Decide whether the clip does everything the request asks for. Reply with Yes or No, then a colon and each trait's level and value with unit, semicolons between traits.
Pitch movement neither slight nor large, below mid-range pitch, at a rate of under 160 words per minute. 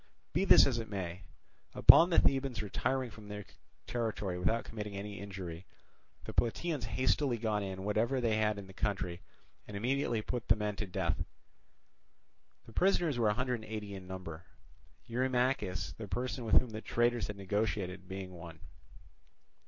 No: average, 3.9 semitones; low, 105 Hz; average, 165 wpm